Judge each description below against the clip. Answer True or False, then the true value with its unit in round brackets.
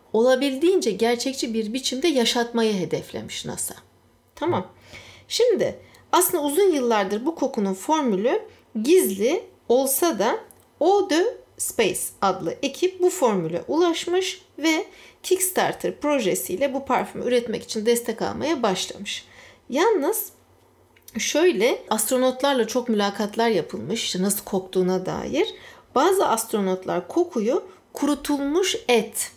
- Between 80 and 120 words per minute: True (100 wpm)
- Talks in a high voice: True (275 Hz)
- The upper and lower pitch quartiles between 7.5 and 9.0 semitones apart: True (8.2 semitones)